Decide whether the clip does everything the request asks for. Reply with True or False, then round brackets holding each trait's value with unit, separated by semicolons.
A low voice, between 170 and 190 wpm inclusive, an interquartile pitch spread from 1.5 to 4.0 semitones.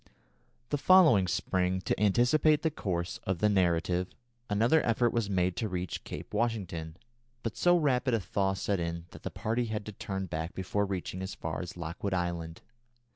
False (95 Hz; 180 wpm; 4.6 semitones)